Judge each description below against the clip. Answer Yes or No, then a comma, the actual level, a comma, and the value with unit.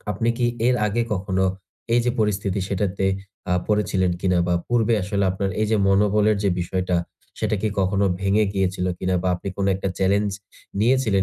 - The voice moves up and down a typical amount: No, narrow, 2.0 semitones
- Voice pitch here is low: Yes, low, 100 Hz